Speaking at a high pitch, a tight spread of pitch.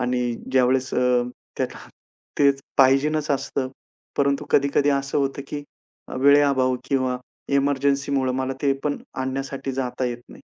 No: low, 135 Hz; narrow, 1.3 semitones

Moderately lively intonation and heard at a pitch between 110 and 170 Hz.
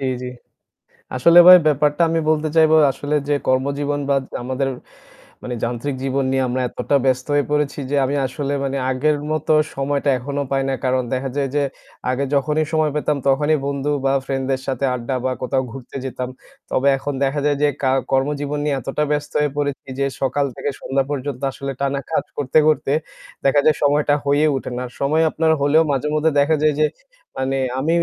No: narrow, 1.9 semitones; medium, 140 Hz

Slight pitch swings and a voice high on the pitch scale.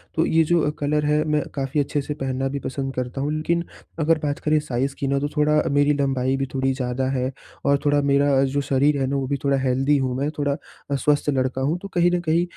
No: narrow, 1.9 semitones; medium, 140 Hz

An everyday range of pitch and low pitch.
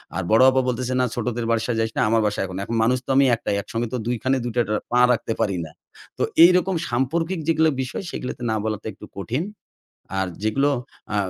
Yes: average, 3.1 semitones; low, 120 Hz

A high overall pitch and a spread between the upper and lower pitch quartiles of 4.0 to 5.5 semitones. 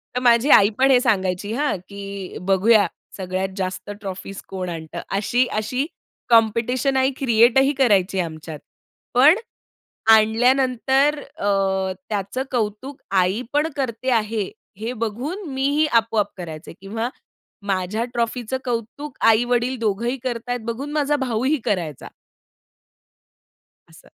Yes: high, 230 Hz; average, 4.7 semitones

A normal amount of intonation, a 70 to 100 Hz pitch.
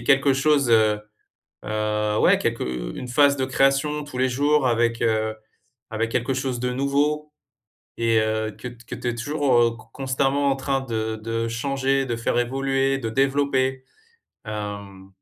No: average, 3.3 semitones; low, 125 Hz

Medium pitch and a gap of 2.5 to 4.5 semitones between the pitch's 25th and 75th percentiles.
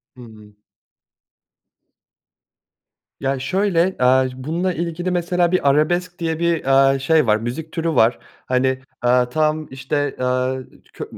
No: medium, 145 Hz; average, 4.9 semitones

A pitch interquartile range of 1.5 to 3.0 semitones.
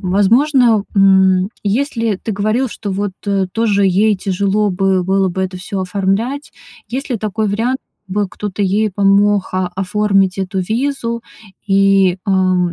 Yes: narrow, 2.4 semitones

